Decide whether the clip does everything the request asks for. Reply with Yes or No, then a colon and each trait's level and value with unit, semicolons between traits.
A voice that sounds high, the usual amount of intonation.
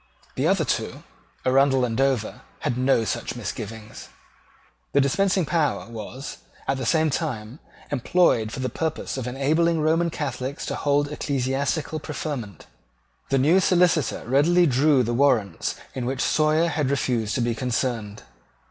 No: low, 135 Hz; average, 4.2 semitones